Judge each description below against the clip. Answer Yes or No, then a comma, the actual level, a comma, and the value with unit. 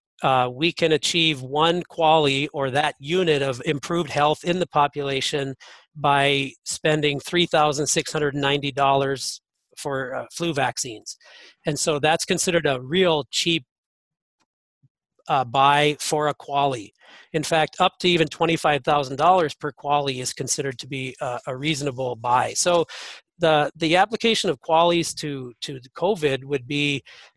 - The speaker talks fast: No, slow, 135 wpm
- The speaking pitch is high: No, medium, 150 Hz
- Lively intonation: No, average, 2.9 semitones